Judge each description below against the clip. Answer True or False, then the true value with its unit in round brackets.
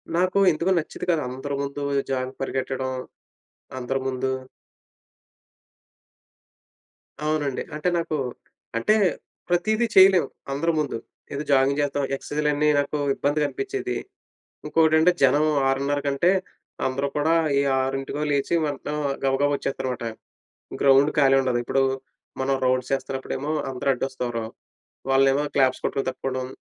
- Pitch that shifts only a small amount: True (2.3 semitones)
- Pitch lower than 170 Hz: True (140 Hz)